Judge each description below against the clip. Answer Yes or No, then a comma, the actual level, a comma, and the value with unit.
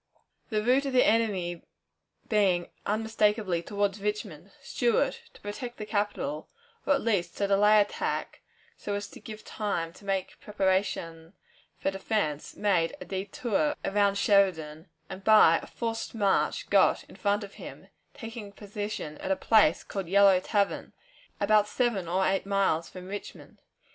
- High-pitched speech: Yes, high, 205 Hz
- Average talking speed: Yes, average, 150 wpm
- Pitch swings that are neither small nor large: No, narrow, 2.2 semitones